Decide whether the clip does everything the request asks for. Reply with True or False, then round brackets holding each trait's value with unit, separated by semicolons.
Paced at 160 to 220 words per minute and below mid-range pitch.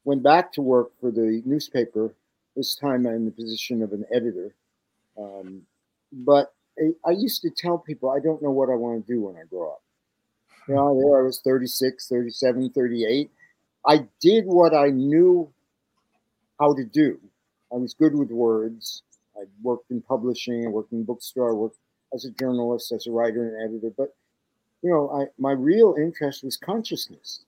True (185 wpm; 130 Hz)